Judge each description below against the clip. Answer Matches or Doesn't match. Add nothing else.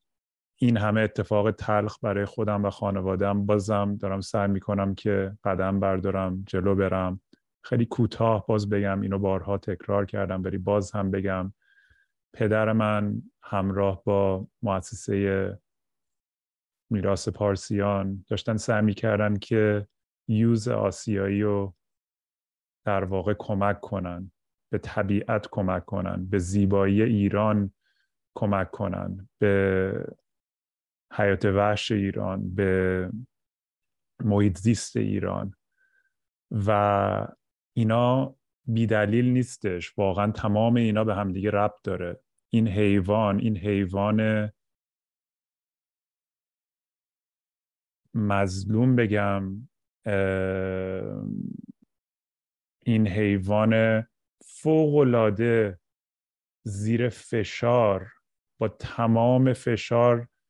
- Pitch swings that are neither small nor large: Doesn't match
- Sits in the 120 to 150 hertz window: Doesn't match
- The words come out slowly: Matches